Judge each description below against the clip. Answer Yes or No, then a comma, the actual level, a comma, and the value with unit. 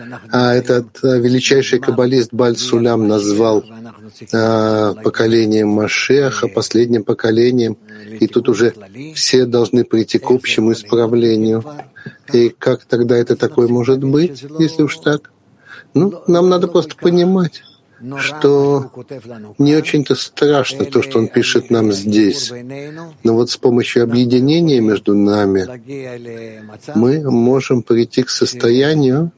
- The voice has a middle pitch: No, low, 120 Hz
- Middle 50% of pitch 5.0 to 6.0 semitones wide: No, average, 3.3 semitones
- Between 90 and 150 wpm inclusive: Yes, average, 120 wpm